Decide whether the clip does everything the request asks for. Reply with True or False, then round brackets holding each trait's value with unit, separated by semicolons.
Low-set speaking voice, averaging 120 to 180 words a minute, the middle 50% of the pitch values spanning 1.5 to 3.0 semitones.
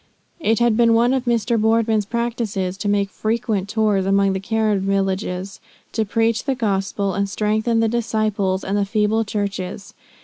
False (215 Hz; 165 wpm; 2.5 semitones)